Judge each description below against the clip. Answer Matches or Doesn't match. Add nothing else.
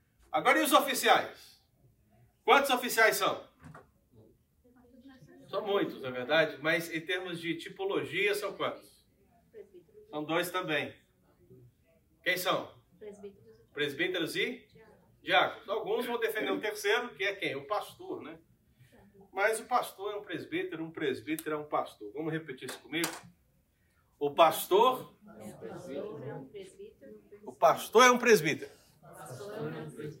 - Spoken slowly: Doesn't match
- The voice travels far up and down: Matches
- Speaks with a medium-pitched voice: Doesn't match